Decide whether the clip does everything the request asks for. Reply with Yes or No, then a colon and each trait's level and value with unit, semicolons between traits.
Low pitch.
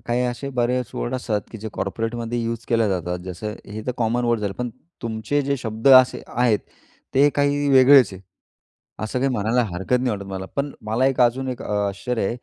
Yes: low, 120 Hz